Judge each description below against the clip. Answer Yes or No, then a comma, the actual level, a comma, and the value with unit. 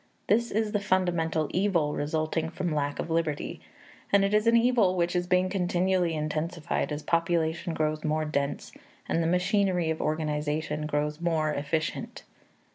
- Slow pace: No, average, 155 wpm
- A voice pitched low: No, medium, 165 Hz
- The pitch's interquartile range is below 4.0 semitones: Yes, average, 3.1 semitones